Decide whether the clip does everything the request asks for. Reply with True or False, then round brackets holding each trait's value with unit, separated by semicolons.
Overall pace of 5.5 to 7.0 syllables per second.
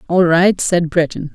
False (4.3 syllables/s)